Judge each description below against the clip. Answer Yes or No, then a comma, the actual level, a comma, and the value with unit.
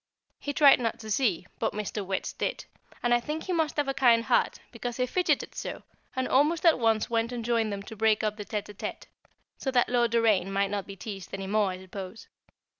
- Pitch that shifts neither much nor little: Yes, average, 3.8 semitones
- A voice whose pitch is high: Yes, high, 225 Hz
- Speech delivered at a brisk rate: Yes, fast, 230 wpm